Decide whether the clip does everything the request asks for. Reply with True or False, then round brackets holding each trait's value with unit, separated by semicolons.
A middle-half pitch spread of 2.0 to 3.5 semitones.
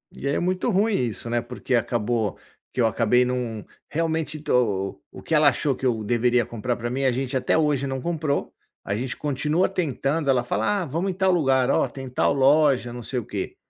False (4.1 semitones)